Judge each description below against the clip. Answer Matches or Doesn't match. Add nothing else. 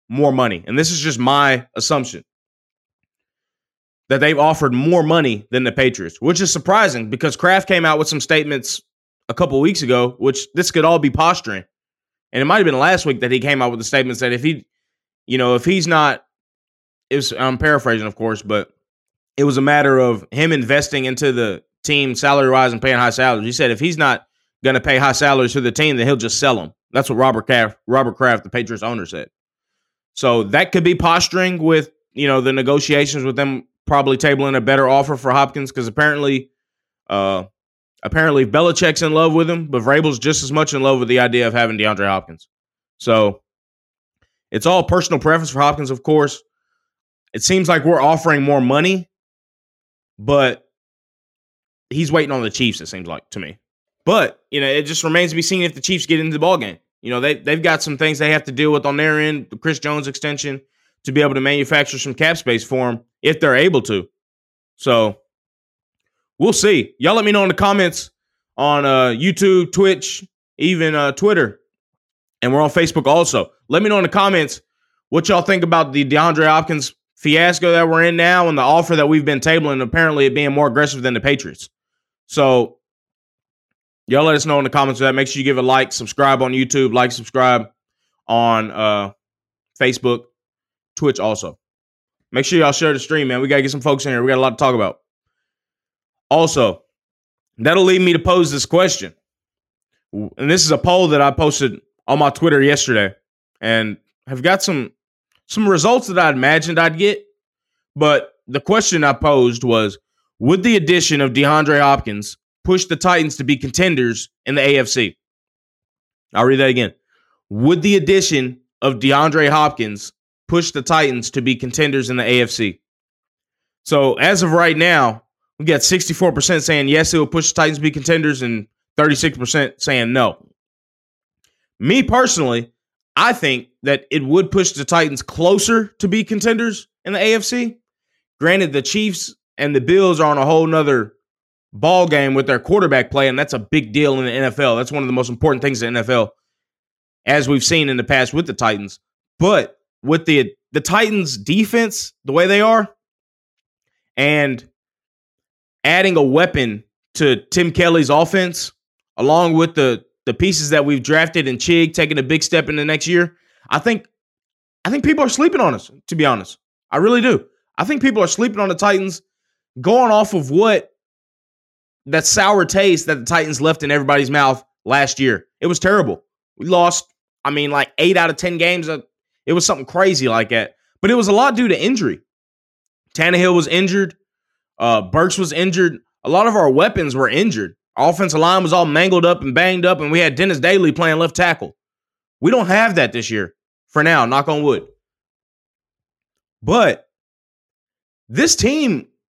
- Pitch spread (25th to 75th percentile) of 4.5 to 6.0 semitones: Matches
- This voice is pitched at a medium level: Matches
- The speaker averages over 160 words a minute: Matches